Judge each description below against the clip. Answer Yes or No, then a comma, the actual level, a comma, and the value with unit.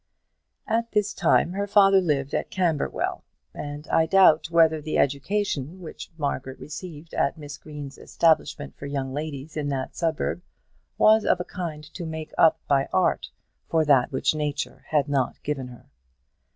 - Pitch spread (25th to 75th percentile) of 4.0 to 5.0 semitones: No, average, 3.2 semitones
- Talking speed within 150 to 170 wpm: Yes, average, 160 wpm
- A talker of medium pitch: Yes, medium, 155 Hz